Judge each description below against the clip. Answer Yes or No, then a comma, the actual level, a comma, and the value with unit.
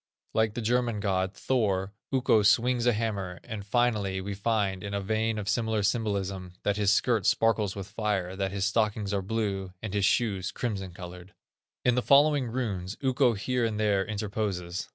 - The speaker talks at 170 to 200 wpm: Yes, average, 175 wpm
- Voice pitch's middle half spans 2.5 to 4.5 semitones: Yes, average, 2.8 semitones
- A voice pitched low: Yes, low, 105 Hz